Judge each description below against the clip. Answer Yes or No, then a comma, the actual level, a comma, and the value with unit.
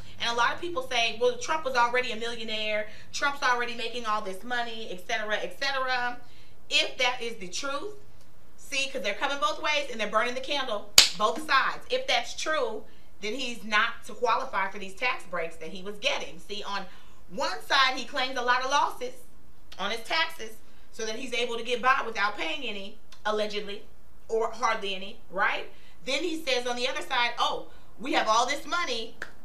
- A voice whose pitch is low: No, high, 240 Hz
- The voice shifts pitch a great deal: No, average, 4.1 semitones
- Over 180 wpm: Yes, average, 200 wpm